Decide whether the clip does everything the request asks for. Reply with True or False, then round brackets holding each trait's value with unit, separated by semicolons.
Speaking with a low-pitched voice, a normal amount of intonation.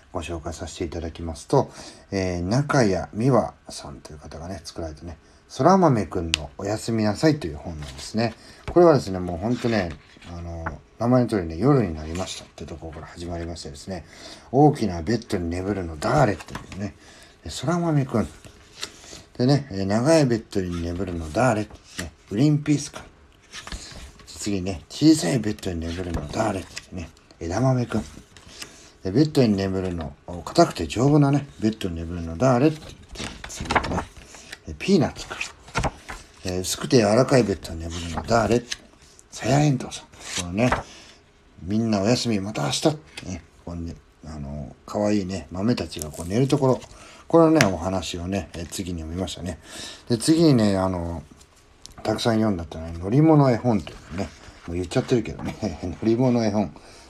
False (95 Hz; 6.0 semitones)